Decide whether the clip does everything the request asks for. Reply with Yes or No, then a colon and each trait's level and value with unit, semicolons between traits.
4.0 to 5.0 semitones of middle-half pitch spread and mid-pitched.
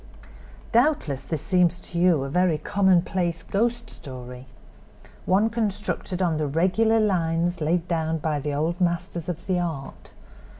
No: average, 3.3 semitones; medium, 175 Hz